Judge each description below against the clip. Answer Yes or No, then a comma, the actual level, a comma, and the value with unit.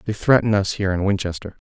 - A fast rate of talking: Yes, fast, 215 wpm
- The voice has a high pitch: No, low, 100 Hz